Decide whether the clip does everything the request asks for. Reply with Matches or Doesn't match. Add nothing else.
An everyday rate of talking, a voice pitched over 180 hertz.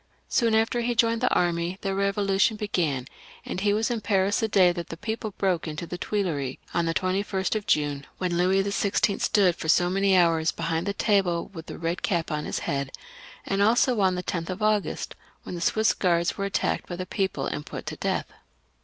Doesn't match